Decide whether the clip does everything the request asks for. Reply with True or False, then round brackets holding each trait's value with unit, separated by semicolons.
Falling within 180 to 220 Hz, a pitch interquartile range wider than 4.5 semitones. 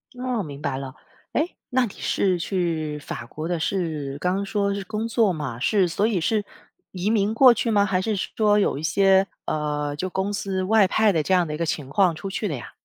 True (190 Hz; 4.9 semitones)